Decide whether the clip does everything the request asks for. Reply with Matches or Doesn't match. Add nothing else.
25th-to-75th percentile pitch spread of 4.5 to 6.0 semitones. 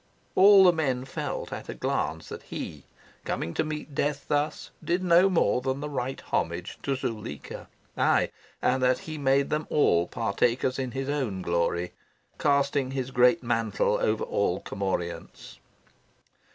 Matches